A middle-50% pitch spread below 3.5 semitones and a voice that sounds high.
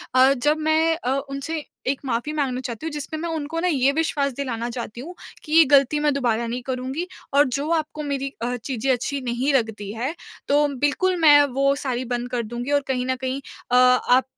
Yes: average, 3.0 semitones; very high, 275 Hz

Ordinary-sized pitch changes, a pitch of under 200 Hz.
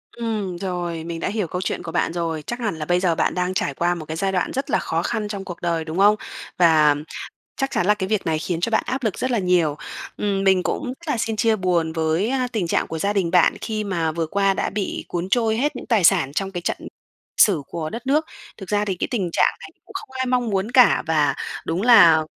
Yes: average, 4.5 semitones; high, 190 Hz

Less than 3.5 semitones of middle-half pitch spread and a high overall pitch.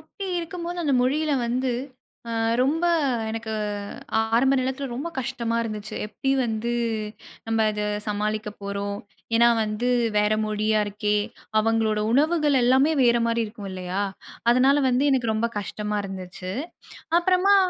No: average, 4.3 semitones; high, 230 Hz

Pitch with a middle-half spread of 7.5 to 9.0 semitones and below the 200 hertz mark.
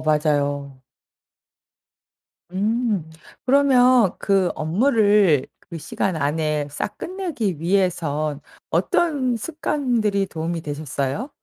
Yes: wide, 8.0 semitones; medium, 185 Hz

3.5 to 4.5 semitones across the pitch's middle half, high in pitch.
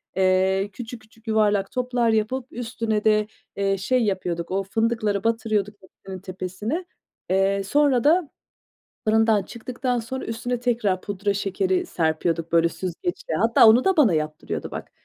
Yes: average, 3.8 semitones; high, 215 Hz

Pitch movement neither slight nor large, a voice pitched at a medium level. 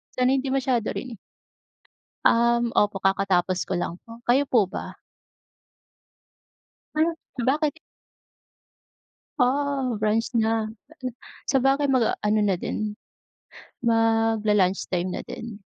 No: average, 3.9 semitones; high, 230 Hz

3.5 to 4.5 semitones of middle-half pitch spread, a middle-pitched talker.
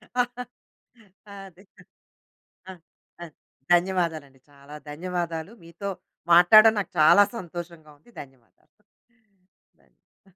Yes: average, 4.2 semitones; medium, 175 Hz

